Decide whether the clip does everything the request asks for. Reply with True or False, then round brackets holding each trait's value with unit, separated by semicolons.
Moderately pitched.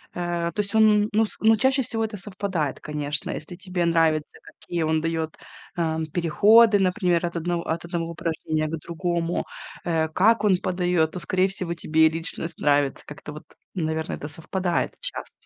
True (170 Hz)